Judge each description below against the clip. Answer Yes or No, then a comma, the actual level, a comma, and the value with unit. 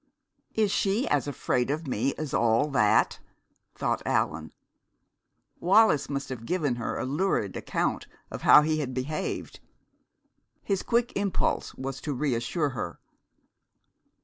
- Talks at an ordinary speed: No, slow, 130 wpm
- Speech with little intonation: No, wide, 5.6 semitones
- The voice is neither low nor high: Yes, medium, 145 Hz